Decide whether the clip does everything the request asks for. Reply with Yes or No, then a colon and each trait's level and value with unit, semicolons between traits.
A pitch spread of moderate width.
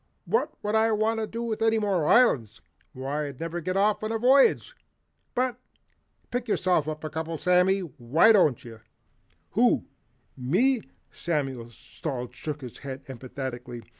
No: wide, 8.6 semitones